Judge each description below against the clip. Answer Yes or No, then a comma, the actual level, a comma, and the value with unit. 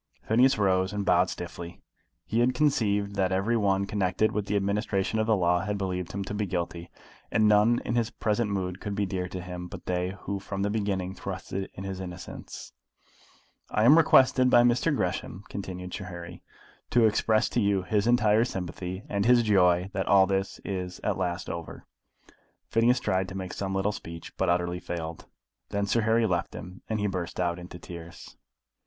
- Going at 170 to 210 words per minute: Yes, average, 190 wpm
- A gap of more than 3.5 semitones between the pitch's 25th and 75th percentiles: No, average, 2.7 semitones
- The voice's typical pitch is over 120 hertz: No, very low, 95 Hz